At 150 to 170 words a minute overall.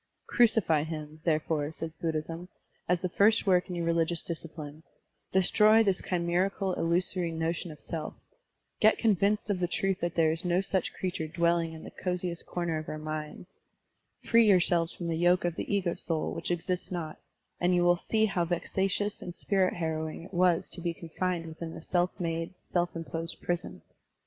No: average, 180 wpm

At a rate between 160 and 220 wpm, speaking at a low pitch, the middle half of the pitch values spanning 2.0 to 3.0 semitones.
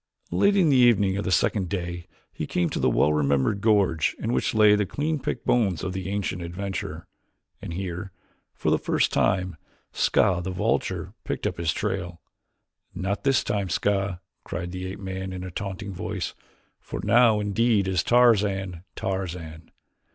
Yes: average, 170 wpm; very low, 95 Hz; average, 2.7 semitones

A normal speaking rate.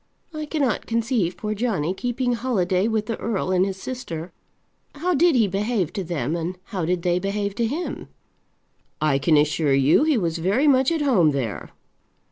Yes: average, 180 wpm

